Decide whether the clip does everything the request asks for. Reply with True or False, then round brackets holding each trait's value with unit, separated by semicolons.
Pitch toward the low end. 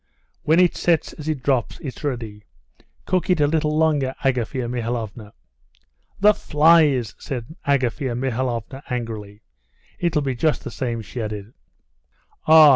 True (130 Hz)